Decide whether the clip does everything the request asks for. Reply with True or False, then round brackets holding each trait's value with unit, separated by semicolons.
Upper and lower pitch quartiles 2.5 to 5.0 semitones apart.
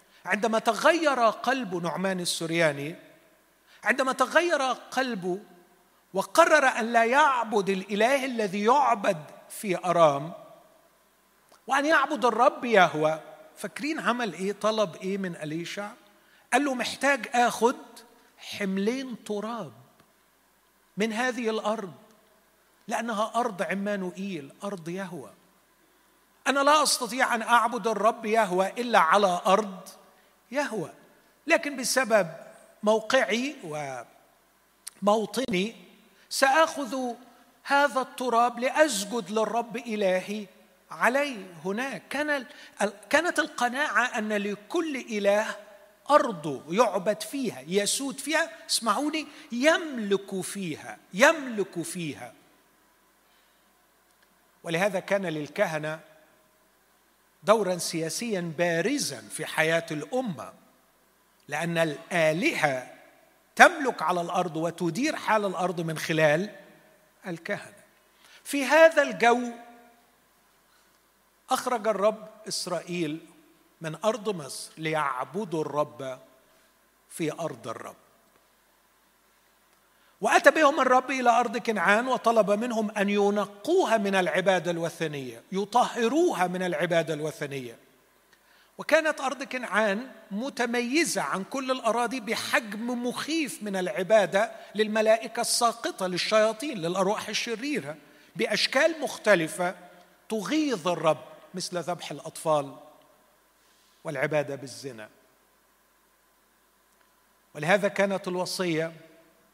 False (5.6 semitones)